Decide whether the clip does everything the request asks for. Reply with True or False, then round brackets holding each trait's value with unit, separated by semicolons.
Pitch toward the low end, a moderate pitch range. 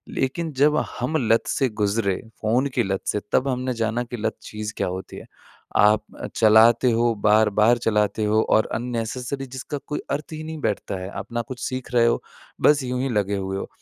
True (115 Hz; 3.3 semitones)